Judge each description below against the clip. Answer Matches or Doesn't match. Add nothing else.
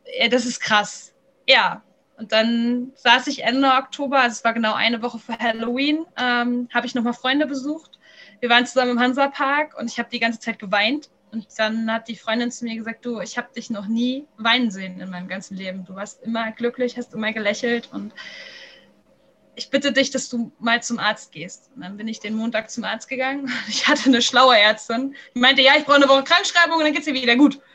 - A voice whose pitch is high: Matches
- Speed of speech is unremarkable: Doesn't match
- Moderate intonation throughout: Matches